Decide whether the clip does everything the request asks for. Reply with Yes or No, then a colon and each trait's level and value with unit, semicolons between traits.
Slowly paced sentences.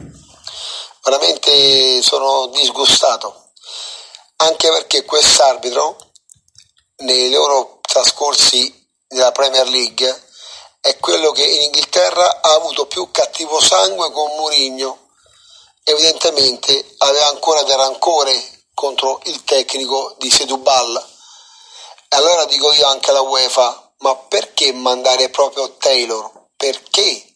Yes: slow, 100 wpm